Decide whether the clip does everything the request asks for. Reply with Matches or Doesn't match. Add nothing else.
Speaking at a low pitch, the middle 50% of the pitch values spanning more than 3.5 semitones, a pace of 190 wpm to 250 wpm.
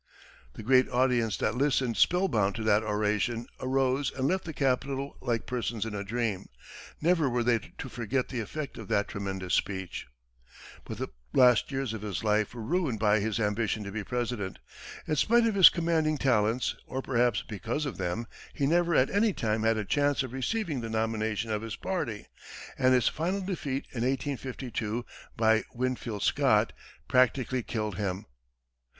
Doesn't match